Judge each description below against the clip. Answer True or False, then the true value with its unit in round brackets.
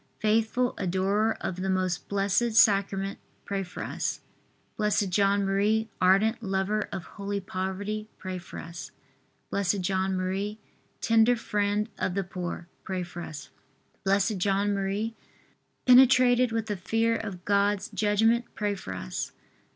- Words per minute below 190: True (135 wpm)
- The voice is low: False (200 Hz)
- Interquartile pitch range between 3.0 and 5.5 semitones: False (2.4 semitones)